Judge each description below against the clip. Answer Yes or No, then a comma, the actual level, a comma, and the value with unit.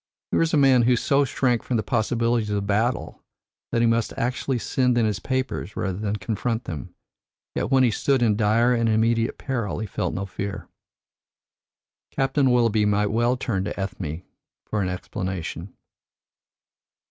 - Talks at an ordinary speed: Yes, average, 165 wpm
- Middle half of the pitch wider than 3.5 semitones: No, average, 3.2 semitones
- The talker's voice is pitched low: Yes, low, 115 Hz